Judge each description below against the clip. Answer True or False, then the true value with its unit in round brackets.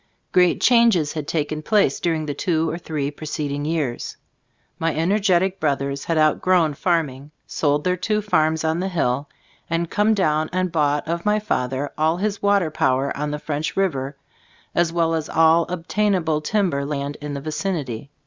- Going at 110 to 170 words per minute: True (165 wpm)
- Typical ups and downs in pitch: True (3.7 semitones)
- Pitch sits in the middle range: True (160 Hz)